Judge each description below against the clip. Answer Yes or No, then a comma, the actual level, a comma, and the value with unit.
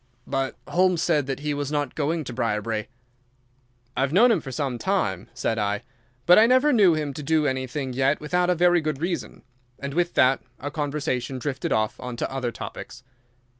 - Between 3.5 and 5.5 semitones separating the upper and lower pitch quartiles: Yes, average, 4.7 semitones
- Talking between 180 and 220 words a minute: Yes, average, 190 wpm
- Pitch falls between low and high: Yes, medium, 145 Hz